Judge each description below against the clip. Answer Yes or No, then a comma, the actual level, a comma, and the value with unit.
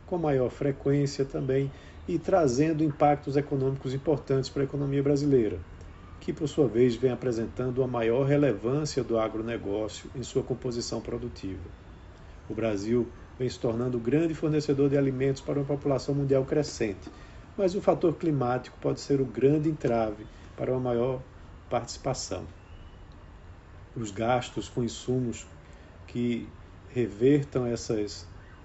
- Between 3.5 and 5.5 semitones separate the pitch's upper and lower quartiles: Yes, average, 4.2 semitones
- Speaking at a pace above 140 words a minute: No, average, 130 wpm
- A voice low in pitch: Yes, low, 125 Hz